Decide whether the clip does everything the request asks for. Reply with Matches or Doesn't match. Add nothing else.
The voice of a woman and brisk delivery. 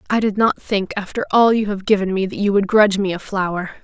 Matches